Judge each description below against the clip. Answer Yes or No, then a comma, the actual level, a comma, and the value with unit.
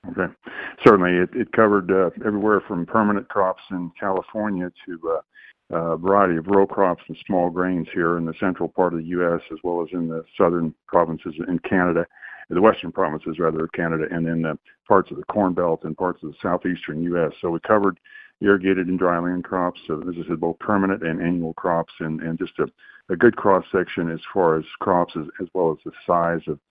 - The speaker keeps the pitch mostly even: Yes, narrow, 2.3 semitones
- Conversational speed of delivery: No, fast, 210 wpm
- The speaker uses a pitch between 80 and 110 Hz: Yes, very low, 85 Hz